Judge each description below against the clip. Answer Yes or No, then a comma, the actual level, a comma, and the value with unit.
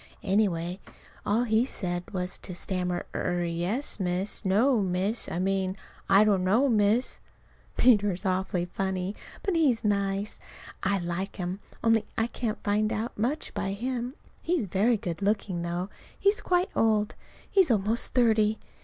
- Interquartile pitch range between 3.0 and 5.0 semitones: Yes, average, 3.6 semitones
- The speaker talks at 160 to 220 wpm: No, average, 150 wpm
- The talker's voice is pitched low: No, high, 205 Hz